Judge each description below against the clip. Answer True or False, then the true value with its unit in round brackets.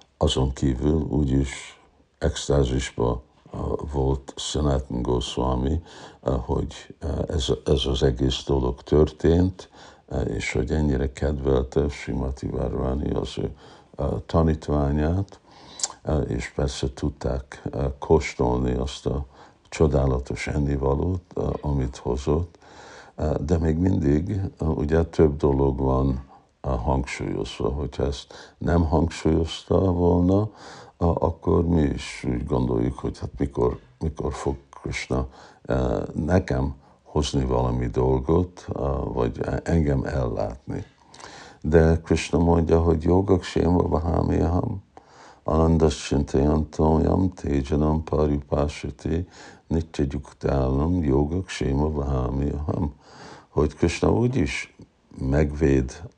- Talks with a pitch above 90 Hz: False (75 Hz)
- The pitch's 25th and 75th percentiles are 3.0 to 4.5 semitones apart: True (3.6 semitones)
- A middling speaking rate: False (100 wpm)